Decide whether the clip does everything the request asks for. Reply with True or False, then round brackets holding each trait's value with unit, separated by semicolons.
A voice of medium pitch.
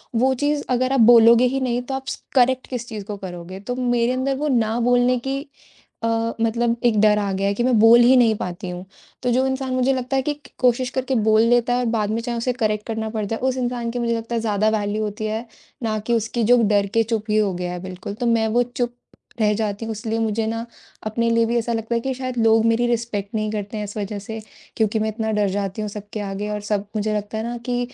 False (230 Hz)